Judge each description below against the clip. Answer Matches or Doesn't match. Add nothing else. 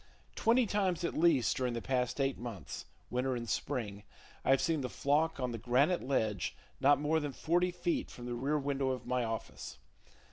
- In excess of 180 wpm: Matches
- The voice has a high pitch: Doesn't match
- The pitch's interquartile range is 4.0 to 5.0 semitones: Matches